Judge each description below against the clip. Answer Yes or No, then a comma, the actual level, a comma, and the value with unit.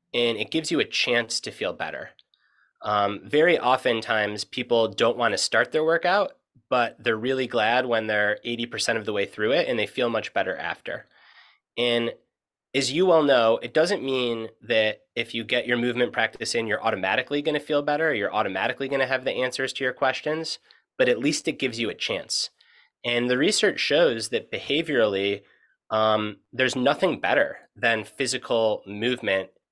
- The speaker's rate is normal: Yes, average, 185 wpm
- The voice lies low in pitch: Yes, low, 120 Hz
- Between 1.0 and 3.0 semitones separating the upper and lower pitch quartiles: No, average, 3.6 semitones